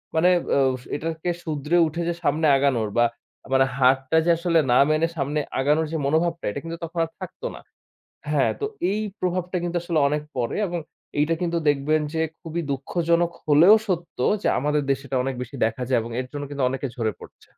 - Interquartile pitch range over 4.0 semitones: No, average, 3.7 semitones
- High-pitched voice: No, medium, 155 Hz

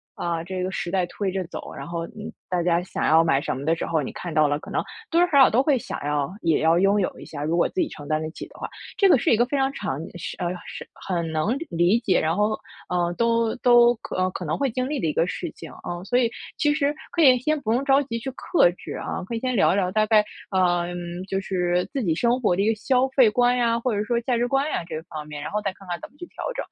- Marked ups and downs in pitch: Yes, wide, 6.2 semitones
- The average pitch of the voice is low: No, high, 195 Hz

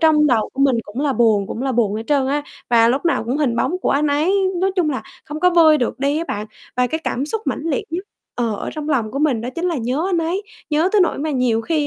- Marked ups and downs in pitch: No, average, 4.7 semitones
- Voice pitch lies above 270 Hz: Yes, very high, 285 Hz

